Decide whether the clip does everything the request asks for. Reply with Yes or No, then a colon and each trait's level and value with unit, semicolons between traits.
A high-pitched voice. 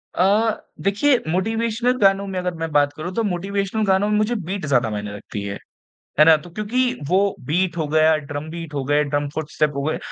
No: medium, 175 Hz